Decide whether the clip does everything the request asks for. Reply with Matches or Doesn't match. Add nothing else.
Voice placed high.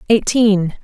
Matches